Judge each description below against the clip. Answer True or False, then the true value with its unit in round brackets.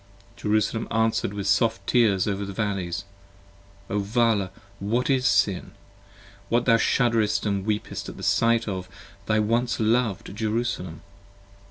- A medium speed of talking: False (125 wpm)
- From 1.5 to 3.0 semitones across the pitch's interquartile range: True (2.7 semitones)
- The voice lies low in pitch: True (110 Hz)